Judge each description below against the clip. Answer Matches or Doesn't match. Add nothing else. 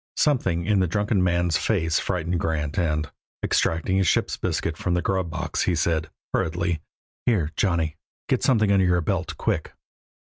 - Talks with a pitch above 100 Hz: Doesn't match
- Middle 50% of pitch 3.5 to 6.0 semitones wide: Doesn't match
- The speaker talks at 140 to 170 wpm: Matches